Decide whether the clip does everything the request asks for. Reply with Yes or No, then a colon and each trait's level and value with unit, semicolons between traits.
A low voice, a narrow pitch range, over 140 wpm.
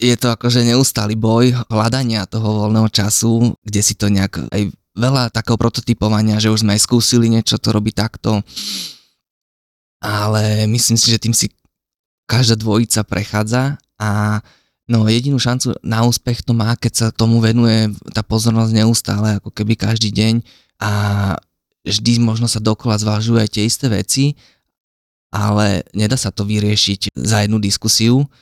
Yes: low, 110 Hz; narrow, 1.8 semitones; average, 150 wpm